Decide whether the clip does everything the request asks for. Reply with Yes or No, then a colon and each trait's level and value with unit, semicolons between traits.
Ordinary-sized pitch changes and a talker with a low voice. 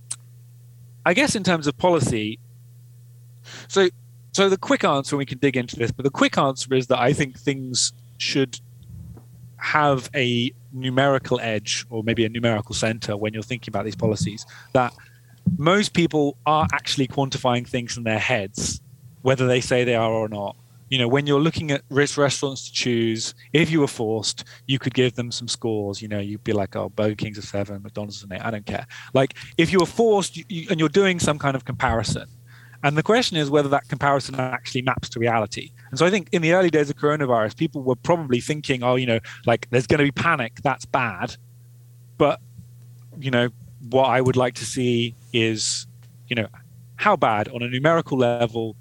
Yes: average, 3.0 semitones; low, 125 Hz